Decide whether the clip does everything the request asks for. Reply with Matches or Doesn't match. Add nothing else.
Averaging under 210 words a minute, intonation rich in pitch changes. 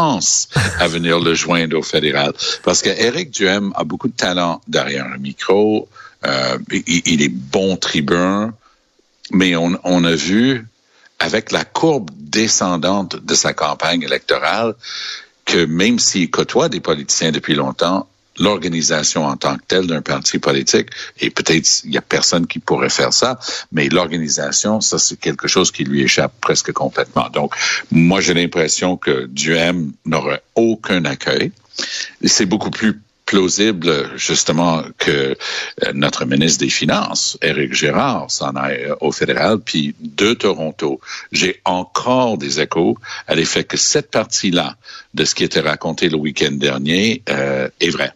Doesn't match